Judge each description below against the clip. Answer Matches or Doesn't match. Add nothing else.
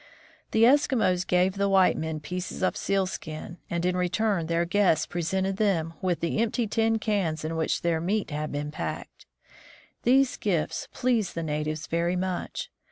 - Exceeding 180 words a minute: Doesn't match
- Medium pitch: Matches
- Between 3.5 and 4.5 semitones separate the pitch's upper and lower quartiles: Matches